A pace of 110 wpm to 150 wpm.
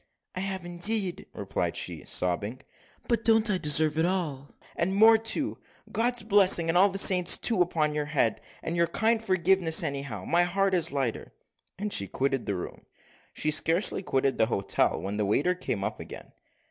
No: average, 185 wpm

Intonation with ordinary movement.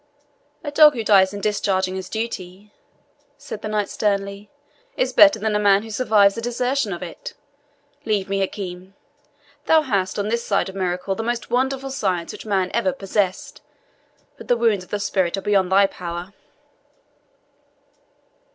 Yes: average, 3.3 semitones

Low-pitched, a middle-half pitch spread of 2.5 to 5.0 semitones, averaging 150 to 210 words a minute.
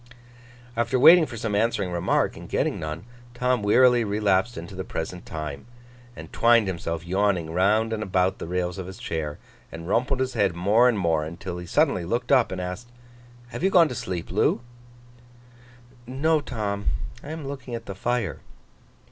No: low, 100 Hz; wide, 5.4 semitones; average, 175 wpm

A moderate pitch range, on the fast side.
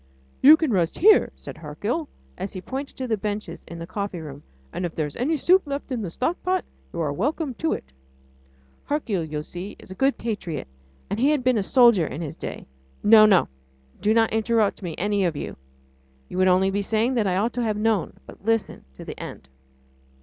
No: wide, 5.9 semitones; fast, 215 wpm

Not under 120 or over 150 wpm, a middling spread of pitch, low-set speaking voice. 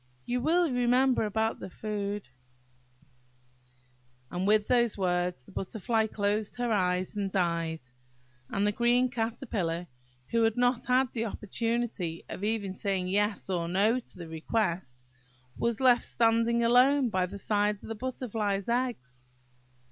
No: average, 140 wpm; average, 4.1 semitones; high, 215 Hz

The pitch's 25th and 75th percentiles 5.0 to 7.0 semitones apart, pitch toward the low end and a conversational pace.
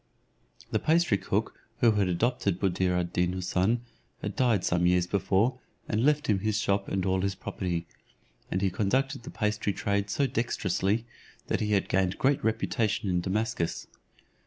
No: average, 3.5 semitones; low, 100 Hz; average, 165 wpm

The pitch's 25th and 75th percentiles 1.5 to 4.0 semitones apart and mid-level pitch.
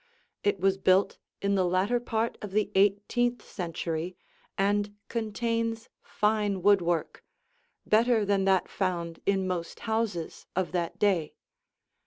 No: average, 2.9 semitones; high, 200 Hz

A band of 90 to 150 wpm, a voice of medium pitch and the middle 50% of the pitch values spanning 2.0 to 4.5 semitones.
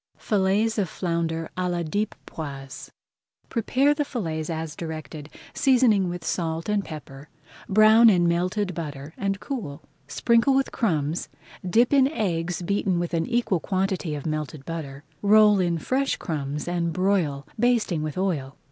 No: average, 145 wpm; medium, 175 Hz; average, 5.0 semitones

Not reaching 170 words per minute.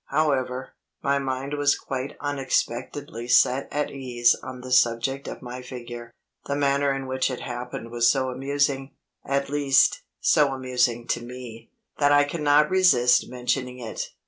Yes: average, 150 wpm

